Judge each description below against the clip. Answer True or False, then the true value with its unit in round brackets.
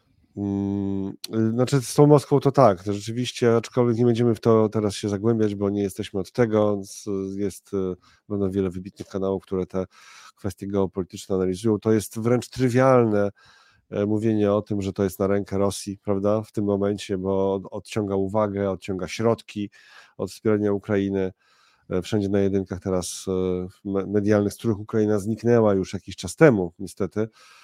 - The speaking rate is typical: True (150 wpm)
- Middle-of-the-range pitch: False (100 Hz)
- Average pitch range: False (2.2 semitones)